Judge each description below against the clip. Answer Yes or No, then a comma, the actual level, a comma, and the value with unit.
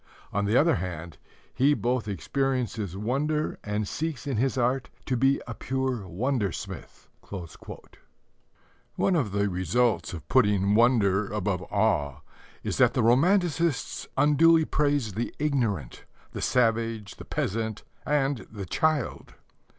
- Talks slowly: Yes, slow, 130 wpm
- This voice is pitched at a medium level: No, low, 120 Hz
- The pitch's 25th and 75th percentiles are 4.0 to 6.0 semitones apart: Yes, average, 5.2 semitones